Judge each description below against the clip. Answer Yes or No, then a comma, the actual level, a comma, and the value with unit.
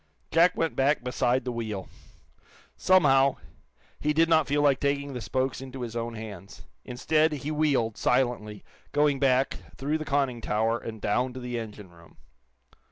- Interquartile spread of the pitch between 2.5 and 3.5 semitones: No, average, 3.9 semitones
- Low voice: Yes, low, 130 Hz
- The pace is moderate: Yes, average, 165 wpm